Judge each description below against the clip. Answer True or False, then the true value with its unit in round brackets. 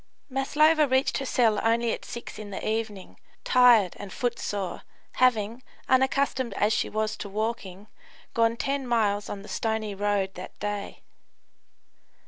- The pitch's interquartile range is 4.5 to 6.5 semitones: False (3.5 semitones)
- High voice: True (220 Hz)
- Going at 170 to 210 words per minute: False (140 wpm)